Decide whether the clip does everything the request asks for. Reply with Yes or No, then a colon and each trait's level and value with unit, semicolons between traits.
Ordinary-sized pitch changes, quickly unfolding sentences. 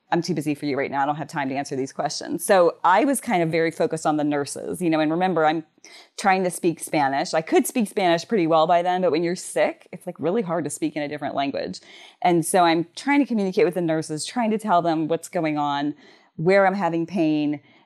Yes: average, 3.4 semitones; fast, 255 wpm